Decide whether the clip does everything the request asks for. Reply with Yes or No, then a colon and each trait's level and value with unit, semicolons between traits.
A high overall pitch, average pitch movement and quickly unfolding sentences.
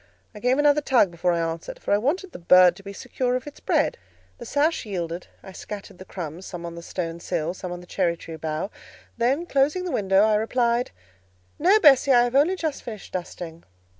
No: high, 205 Hz; wide, 7.5 semitones; fast, 215 wpm